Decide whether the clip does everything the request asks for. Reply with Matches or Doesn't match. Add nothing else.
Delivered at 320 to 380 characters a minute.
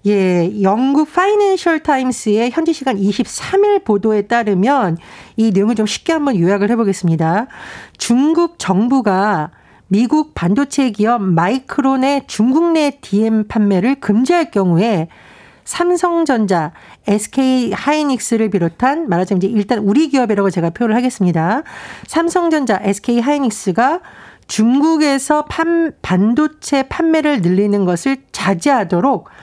Doesn't match